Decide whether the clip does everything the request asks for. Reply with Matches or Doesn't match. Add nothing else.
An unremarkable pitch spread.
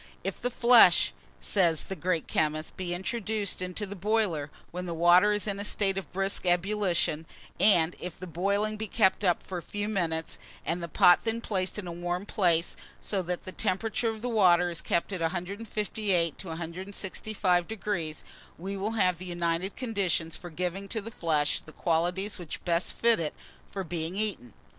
Matches